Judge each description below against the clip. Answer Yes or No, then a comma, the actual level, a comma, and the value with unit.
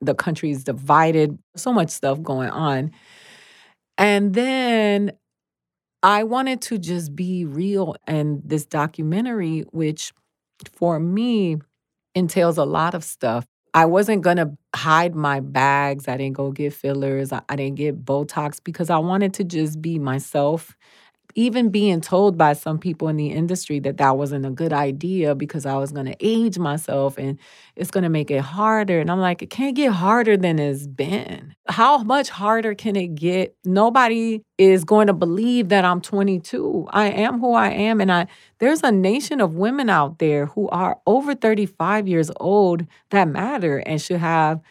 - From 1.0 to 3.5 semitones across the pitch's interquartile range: No, wide, 5.6 semitones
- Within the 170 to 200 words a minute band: Yes, average, 175 wpm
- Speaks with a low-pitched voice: No, medium, 170 Hz